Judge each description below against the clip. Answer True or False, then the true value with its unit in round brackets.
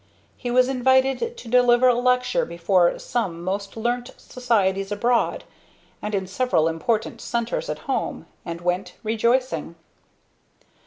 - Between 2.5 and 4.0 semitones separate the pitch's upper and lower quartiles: False (4.6 semitones)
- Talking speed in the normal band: False (125 wpm)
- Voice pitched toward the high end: True (235 Hz)